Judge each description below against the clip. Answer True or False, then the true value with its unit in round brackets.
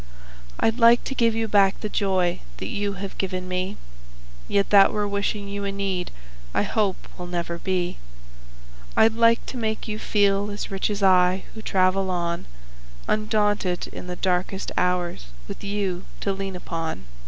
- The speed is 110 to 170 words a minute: True (165 wpm)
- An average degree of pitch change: False (2.3 semitones)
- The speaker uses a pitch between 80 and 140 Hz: False (195 Hz)